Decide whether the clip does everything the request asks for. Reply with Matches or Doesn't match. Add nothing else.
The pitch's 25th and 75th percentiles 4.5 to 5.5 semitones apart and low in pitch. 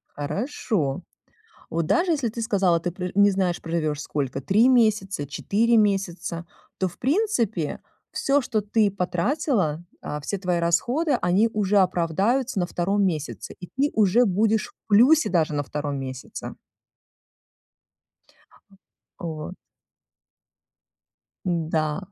Doesn't match